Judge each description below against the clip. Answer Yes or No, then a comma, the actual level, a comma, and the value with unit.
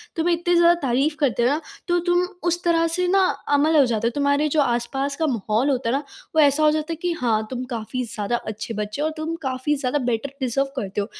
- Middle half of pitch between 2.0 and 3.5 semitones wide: No, average, 4.8 semitones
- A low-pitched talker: No, very high, 280 Hz